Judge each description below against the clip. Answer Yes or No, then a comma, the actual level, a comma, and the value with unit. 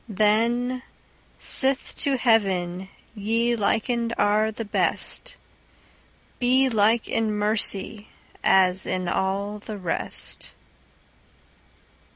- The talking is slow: Yes, slow, 85 wpm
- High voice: Yes, high, 215 Hz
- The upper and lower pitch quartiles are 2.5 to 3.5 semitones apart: Yes, average, 2.9 semitones